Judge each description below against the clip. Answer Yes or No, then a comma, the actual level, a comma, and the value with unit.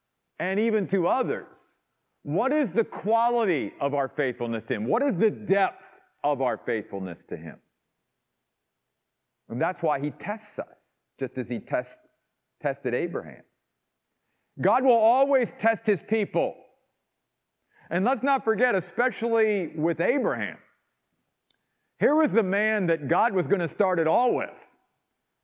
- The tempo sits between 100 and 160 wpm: Yes, average, 140 wpm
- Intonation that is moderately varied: No, wide, 6.0 semitones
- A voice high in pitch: Yes, high, 205 Hz